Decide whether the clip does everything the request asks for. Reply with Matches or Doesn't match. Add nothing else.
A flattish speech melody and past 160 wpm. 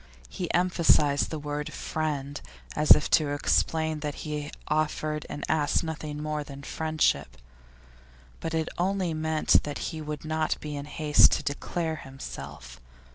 Doesn't match